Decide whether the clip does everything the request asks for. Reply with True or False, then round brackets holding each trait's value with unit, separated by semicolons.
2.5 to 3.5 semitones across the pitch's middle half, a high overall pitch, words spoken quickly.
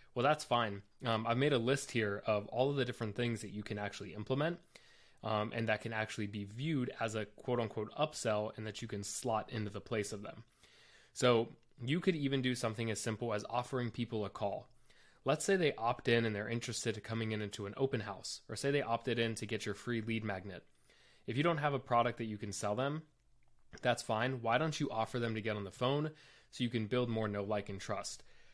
False (3.0 semitones; 115 Hz; 240 wpm)